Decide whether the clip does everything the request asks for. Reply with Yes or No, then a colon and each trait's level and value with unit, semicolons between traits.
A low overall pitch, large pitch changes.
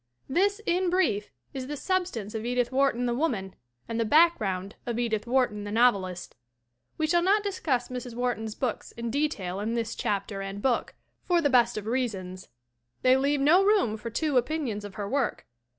No: high, 245 Hz; wide, 5.7 semitones